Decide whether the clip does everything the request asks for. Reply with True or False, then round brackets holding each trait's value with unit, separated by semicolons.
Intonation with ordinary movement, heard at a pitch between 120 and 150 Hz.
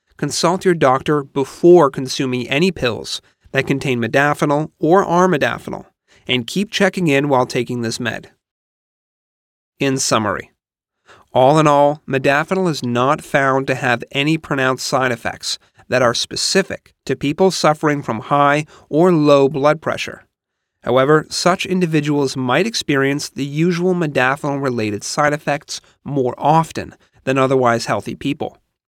True (3.4 semitones; 140 Hz)